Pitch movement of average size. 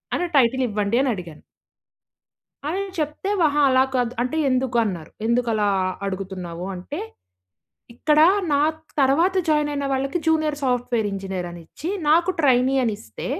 No: wide, 6.5 semitones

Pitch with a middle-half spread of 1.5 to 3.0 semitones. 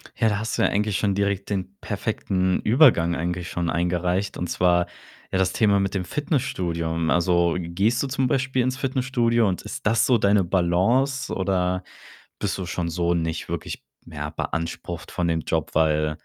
No: average, 4.1 semitones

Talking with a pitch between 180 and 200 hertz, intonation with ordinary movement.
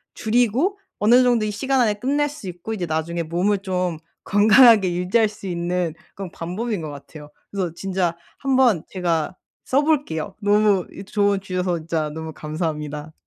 Yes: high, 190 Hz; average, 4.5 semitones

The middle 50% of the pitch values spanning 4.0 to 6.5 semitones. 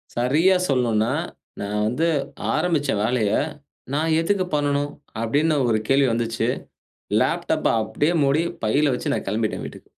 Yes: average, 5.0 semitones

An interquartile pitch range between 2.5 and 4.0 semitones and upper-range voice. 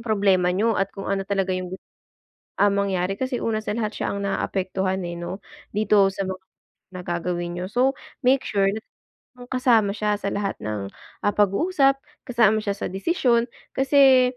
Yes: average, 3.6 semitones; high, 200 Hz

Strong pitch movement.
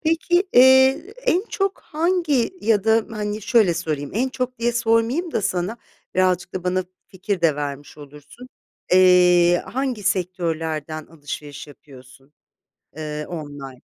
Yes: wide, 8.1 semitones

